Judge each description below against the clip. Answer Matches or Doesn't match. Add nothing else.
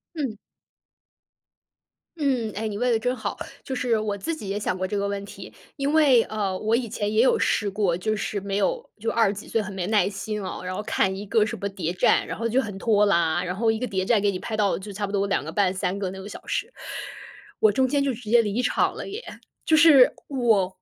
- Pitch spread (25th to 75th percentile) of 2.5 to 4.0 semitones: Matches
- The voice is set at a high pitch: Matches